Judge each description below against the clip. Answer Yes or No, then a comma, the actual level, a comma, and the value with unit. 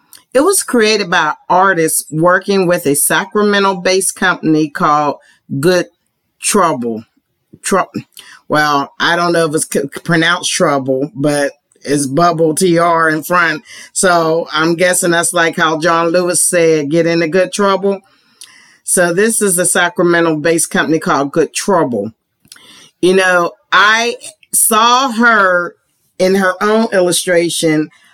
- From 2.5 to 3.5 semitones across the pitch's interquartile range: Yes, average, 2.8 semitones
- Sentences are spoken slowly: Yes, slow, 130 wpm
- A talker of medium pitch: Yes, medium, 175 Hz